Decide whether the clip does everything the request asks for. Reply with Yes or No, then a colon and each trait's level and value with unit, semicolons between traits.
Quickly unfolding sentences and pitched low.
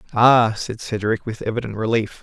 No: average, 160 wpm; low, 110 Hz